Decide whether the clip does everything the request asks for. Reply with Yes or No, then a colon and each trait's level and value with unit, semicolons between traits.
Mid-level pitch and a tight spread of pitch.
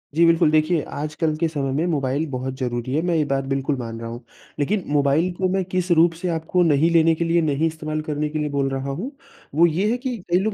No: medium, 155 Hz; average, 3.6 semitones